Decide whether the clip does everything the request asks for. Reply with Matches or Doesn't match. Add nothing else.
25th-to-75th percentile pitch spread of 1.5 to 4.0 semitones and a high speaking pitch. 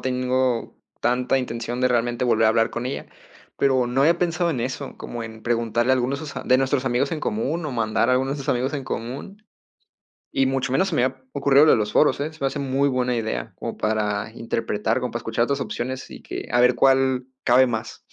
Doesn't match